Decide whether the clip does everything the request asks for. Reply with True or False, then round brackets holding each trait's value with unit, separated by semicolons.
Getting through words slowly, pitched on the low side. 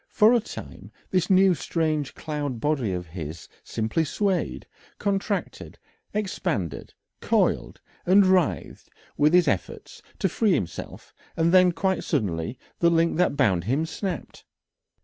False (130 wpm; 165 Hz)